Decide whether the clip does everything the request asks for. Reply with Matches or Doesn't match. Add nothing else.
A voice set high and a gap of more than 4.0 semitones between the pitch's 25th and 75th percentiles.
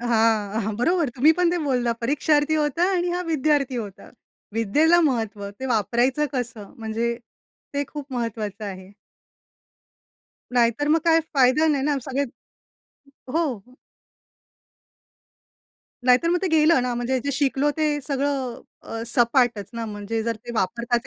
Matches